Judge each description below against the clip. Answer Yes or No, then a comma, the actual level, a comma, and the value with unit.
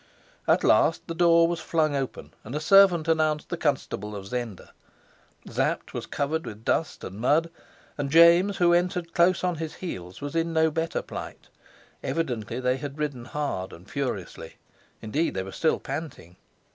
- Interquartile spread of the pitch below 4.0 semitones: No, average, 5.1 semitones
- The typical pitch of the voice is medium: Yes, medium, 155 Hz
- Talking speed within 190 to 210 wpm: No, average, 170 wpm